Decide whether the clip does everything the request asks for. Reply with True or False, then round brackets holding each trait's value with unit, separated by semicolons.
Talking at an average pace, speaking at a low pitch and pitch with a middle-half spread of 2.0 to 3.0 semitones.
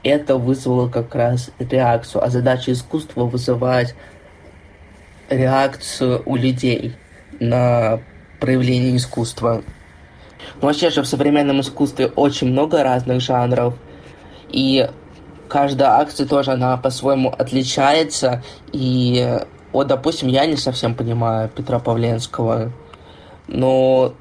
False (105 wpm; 125 Hz; 2.5 semitones)